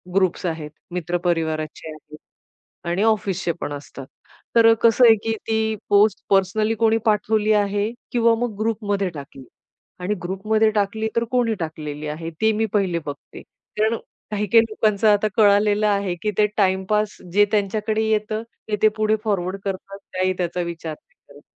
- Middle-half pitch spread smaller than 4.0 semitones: Yes, average, 3.6 semitones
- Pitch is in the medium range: No, high, 205 Hz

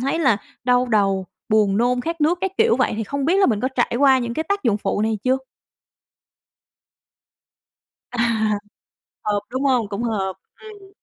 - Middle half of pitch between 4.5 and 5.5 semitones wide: Yes, average, 4.9 semitones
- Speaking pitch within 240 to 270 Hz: Yes, high, 245 Hz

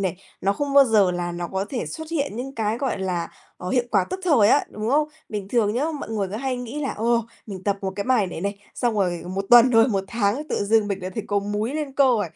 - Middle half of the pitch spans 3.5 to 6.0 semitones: Yes, average, 4.6 semitones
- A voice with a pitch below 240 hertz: Yes, high, 220 Hz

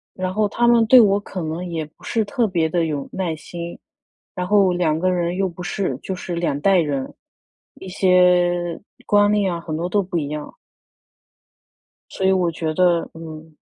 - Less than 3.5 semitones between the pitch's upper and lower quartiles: Yes, average, 2.8 semitones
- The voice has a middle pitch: Yes, medium, 180 Hz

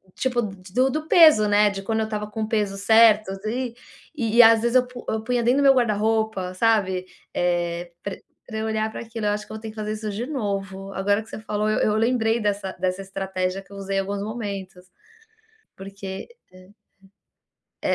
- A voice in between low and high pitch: No, high, 210 Hz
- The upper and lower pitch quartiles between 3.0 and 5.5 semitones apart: No, narrow, 2.5 semitones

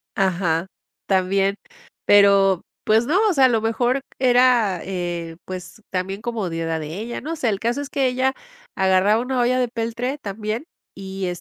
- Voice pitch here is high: Yes, high, 210 Hz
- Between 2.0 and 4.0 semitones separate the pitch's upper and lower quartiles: No, average, 4.7 semitones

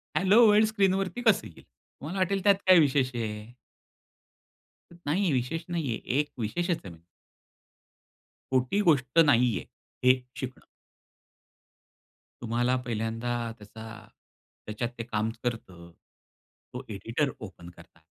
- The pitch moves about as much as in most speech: No, wide, 7.6 semitones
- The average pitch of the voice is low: Yes, low, 125 Hz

